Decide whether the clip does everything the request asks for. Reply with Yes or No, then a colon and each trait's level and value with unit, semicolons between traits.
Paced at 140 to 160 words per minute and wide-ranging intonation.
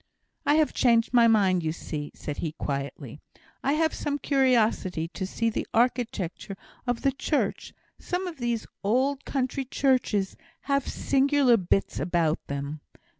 Yes: average, 145 wpm; wide, 7.3 semitones